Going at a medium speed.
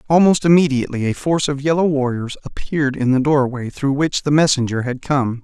Yes: average, 190 wpm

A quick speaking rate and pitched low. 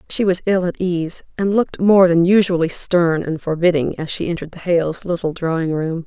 No: fast, 210 wpm; medium, 175 Hz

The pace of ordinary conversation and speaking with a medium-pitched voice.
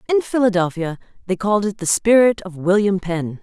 No: average, 175 wpm; high, 195 Hz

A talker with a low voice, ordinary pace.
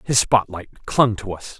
Yes: low, 105 Hz; average, 190 wpm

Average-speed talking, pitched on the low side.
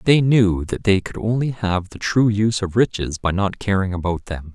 No: fast, 225 wpm; low, 100 Hz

